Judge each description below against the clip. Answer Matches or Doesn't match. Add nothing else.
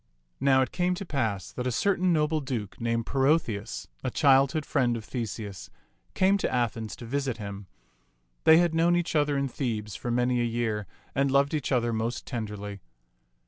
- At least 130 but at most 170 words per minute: Doesn't match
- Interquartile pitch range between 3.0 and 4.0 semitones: Doesn't match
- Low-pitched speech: Matches